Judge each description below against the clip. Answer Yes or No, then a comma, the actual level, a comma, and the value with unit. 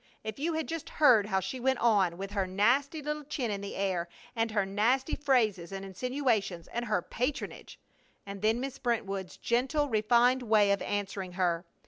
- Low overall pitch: No, high, 220 Hz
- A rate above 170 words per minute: Yes, average, 180 wpm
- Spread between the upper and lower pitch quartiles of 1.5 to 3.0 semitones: No, average, 4.8 semitones